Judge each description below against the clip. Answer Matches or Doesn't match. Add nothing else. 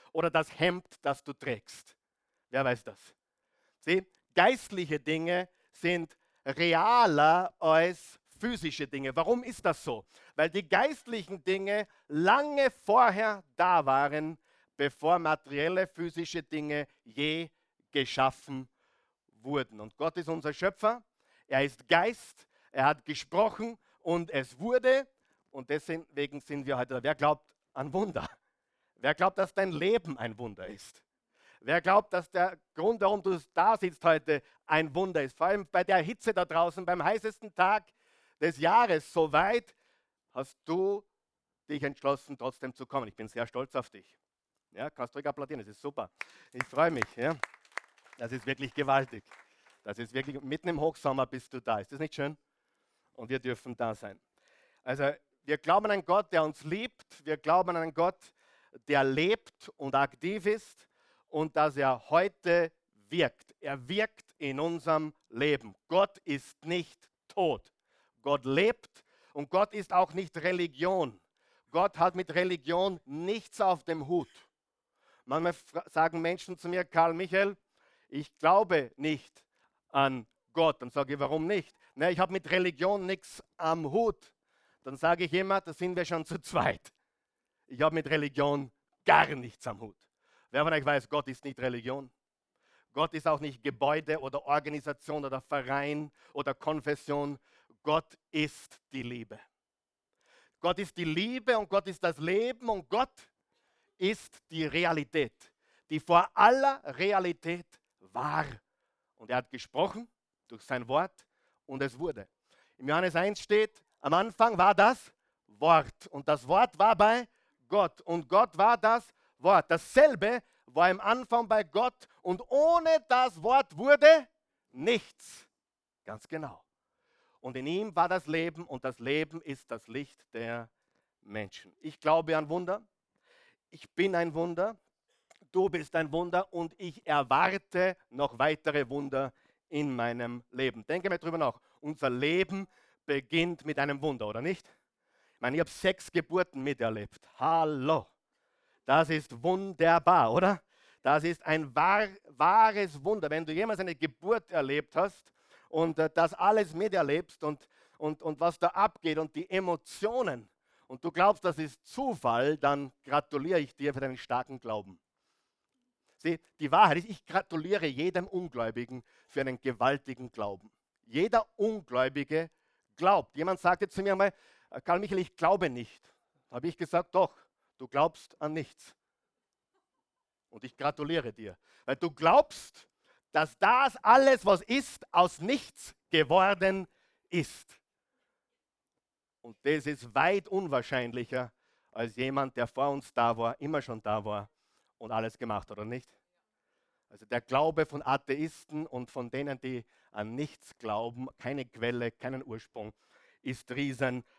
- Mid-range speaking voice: Matches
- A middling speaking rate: Matches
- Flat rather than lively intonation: Doesn't match